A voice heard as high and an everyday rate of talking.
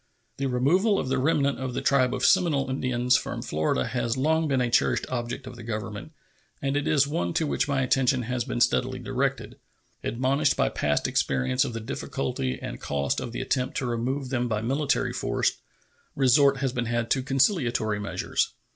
No: low, 130 Hz; average, 190 wpm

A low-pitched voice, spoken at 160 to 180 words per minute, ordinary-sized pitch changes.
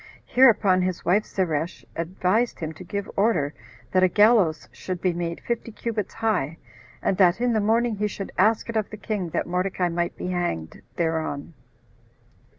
No: medium, 185 Hz; average, 170 wpm; average, 3.8 semitones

